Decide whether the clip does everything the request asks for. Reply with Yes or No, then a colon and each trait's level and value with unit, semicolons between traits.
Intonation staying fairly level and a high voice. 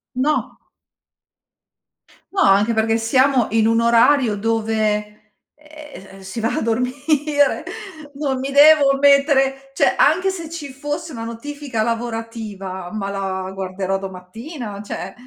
No: average, 5.2 semitones; high, 230 Hz